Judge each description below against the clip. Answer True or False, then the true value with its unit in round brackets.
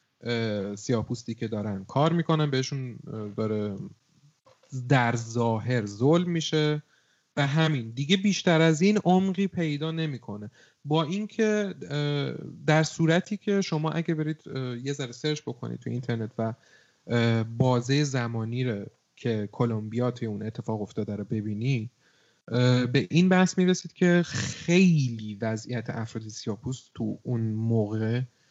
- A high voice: False (130 Hz)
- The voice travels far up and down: True (5.8 semitones)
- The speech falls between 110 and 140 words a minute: True (120 wpm)